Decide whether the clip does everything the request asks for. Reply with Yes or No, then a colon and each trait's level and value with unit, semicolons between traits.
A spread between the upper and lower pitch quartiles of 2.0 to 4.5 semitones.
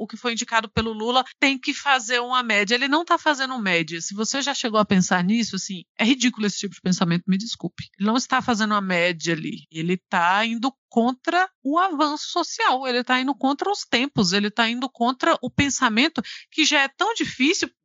No: average, 5.2 semitones